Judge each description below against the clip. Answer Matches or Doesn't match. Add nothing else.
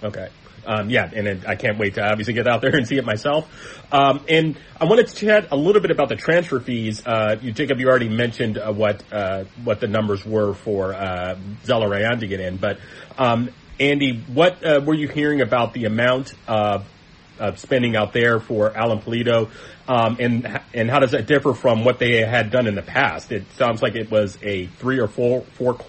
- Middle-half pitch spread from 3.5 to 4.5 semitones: Matches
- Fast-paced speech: Matches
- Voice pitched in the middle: Doesn't match